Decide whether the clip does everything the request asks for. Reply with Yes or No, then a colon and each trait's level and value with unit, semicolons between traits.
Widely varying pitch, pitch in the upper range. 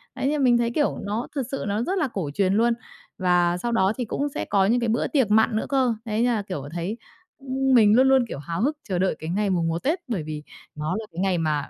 Yes: wide, 5.9 semitones; high, 215 Hz